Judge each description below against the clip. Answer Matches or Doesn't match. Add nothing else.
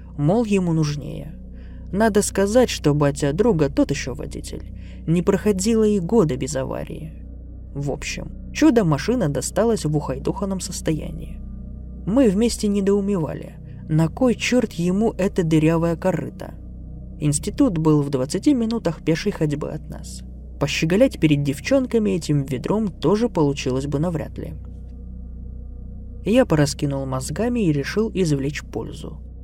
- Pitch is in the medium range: Matches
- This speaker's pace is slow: Doesn't match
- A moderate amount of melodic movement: Doesn't match